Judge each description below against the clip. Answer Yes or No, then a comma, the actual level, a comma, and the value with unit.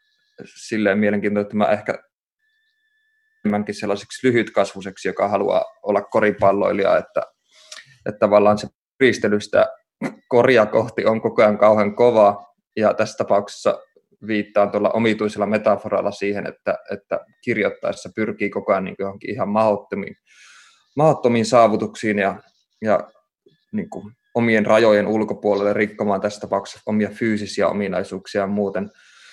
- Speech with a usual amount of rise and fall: No, narrow, 1.9 semitones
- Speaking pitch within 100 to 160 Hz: Yes, low, 105 Hz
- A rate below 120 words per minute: Yes, average, 110 wpm